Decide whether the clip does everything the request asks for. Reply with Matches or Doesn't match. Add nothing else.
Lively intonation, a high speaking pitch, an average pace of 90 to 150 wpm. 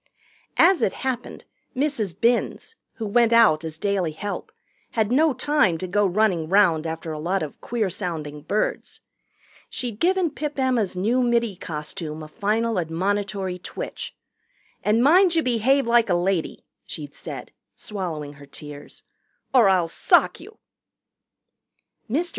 Matches